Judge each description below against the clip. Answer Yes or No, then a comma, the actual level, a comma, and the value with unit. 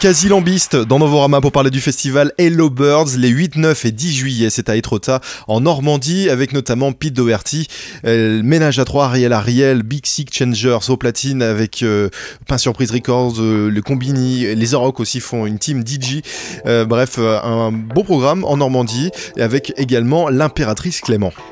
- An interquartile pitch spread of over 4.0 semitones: No, average, 3.7 semitones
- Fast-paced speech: No, average, 180 wpm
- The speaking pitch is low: Yes, low, 130 Hz